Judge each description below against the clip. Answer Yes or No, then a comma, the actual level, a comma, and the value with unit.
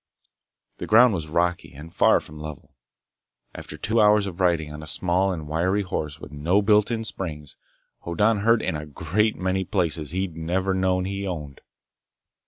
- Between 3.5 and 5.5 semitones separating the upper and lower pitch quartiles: Yes, average, 4.2 semitones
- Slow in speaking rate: No, average, 175 wpm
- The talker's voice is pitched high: No, very low, 90 Hz